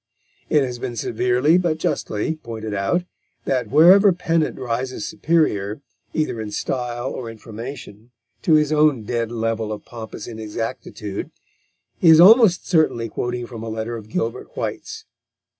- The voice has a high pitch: No, low, 120 Hz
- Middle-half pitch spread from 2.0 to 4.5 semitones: No, wide, 5.6 semitones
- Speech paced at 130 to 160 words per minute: Yes, average, 140 wpm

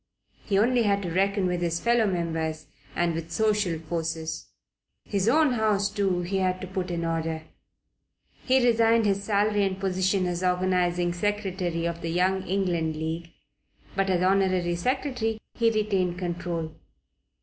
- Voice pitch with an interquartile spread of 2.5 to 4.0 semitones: Yes, average, 3.1 semitones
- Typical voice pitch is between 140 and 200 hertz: Yes, medium, 185 Hz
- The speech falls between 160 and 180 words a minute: No, average, 150 wpm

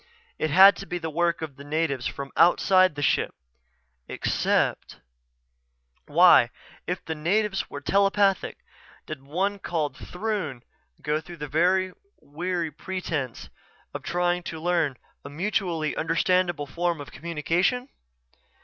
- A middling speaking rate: No, slow, 130 wpm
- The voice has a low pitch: No, medium, 170 Hz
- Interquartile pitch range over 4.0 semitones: No, average, 3.7 semitones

